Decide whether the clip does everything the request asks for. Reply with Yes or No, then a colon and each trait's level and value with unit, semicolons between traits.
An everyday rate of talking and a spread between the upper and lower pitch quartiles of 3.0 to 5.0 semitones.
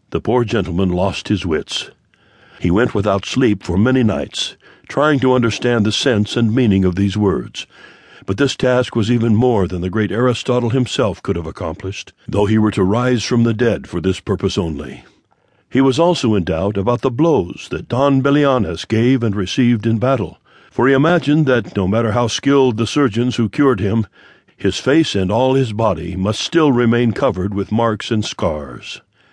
Yes: average, 190 wpm; average, 4.3 semitones